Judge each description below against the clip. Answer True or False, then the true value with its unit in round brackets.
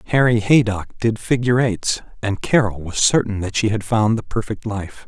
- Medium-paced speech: True (190 wpm)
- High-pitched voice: False (110 Hz)